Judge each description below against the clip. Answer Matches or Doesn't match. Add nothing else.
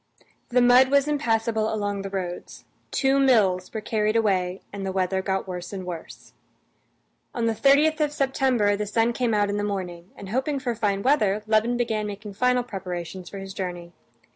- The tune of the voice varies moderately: Matches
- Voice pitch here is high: Matches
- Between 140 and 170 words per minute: Doesn't match